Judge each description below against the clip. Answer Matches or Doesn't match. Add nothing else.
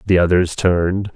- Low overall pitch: Matches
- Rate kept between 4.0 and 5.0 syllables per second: Matches